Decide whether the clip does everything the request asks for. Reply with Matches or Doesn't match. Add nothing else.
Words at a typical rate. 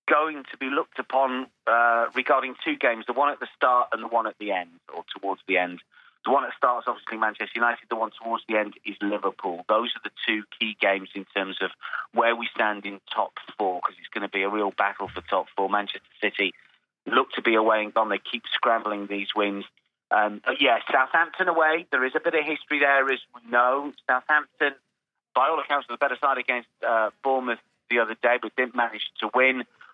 Doesn't match